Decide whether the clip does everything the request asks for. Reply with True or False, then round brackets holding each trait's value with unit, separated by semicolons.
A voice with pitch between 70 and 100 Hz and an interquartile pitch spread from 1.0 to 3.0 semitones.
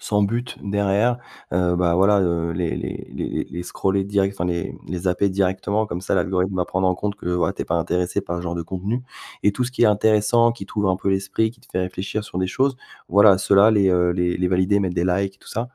True (95 Hz; 2.4 semitones)